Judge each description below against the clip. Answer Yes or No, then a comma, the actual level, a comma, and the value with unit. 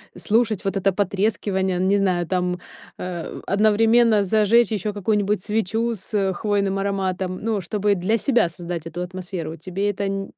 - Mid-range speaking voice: No, high, 195 Hz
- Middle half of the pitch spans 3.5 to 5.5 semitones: No, narrow, 2.5 semitones